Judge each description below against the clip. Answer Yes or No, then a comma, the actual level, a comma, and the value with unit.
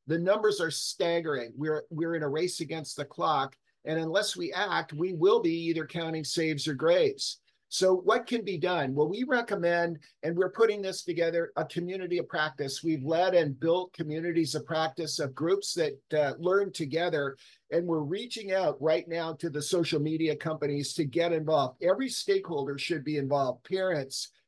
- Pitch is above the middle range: No, medium, 165 Hz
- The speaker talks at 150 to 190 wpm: Yes, average, 180 wpm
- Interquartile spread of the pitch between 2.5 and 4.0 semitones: Yes, average, 3.1 semitones